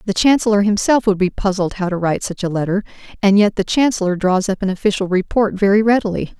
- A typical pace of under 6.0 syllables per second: No, 6.4 syllables/s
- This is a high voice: Yes, high, 200 Hz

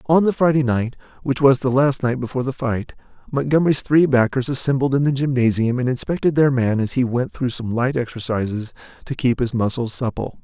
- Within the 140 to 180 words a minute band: No, average, 200 wpm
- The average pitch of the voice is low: Yes, low, 130 Hz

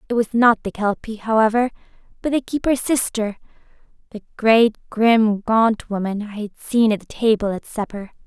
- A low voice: No, high, 220 Hz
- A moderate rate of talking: Yes, average, 165 wpm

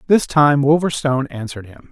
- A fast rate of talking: No, average, 155 wpm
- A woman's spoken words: No, male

